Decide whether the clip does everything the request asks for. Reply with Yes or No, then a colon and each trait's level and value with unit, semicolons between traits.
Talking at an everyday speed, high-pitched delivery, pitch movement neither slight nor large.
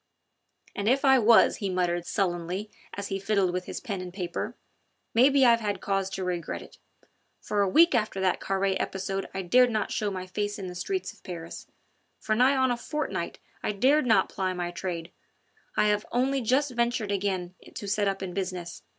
Yes: average, 195 wpm; high, 200 Hz; average, 4.2 semitones